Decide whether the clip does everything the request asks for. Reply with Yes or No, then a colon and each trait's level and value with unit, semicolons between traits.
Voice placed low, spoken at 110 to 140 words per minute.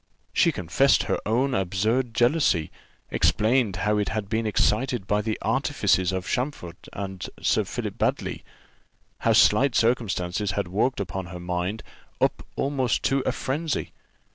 Yes: low, 105 Hz; slow, 135 wpm